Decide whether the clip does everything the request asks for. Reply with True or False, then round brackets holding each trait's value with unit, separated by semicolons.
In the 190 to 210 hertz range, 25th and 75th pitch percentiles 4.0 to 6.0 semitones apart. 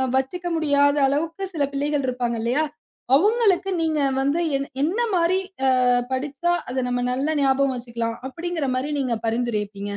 False (280 Hz; 4.6 semitones)